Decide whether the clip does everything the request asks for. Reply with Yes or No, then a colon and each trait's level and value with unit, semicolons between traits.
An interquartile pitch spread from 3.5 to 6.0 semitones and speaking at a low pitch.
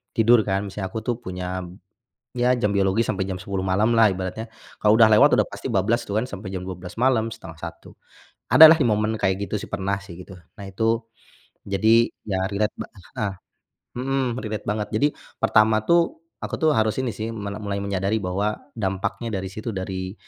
No: average, 2.8 semitones; low, 105 Hz